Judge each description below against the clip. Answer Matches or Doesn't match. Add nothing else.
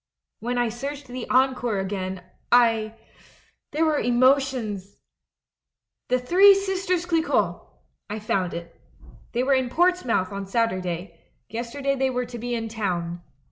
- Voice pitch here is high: Matches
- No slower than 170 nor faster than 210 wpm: Doesn't match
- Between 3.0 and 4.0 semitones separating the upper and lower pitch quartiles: Doesn't match